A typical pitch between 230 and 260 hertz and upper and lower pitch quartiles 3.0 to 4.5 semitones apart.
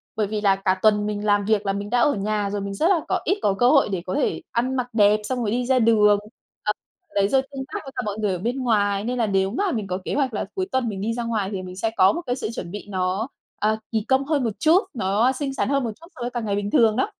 No: high, 215 Hz; average, 4.0 semitones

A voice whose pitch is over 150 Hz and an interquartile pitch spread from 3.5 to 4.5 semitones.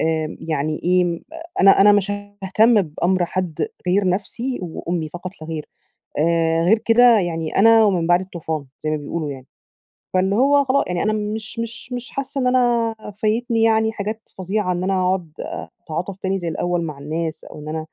No: medium, 185 Hz; average, 5.0 semitones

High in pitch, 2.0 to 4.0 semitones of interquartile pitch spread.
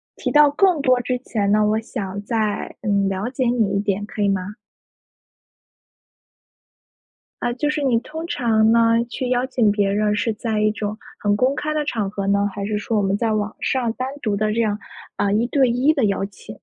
Yes: high, 220 Hz; average, 3.4 semitones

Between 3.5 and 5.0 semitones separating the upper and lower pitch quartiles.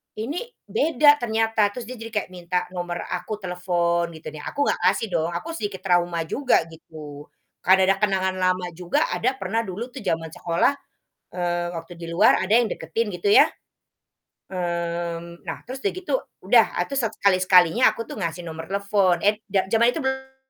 Yes: average, 4.6 semitones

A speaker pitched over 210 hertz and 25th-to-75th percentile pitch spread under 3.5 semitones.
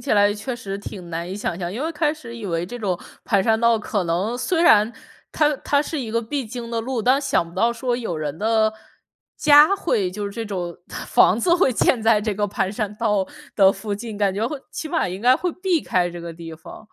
No: high, 220 Hz; average, 4.6 semitones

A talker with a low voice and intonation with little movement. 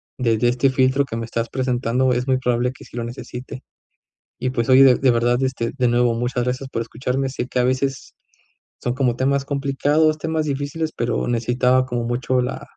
Yes: low, 125 Hz; narrow, 1.9 semitones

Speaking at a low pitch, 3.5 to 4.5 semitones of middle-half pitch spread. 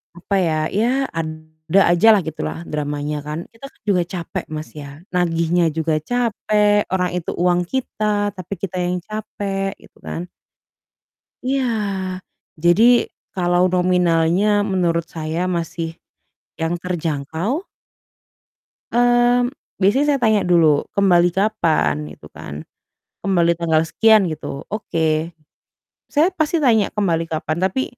No: medium, 180 Hz; average, 4.2 semitones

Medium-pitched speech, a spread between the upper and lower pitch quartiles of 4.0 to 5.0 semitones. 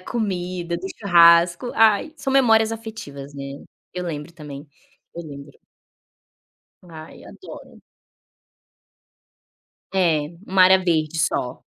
Yes: medium, 175 Hz; average, 4.3 semitones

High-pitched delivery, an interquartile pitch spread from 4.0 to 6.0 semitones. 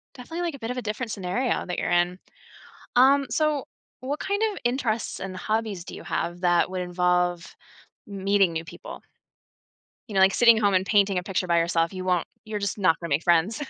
Yes: high, 195 Hz; average, 4.7 semitones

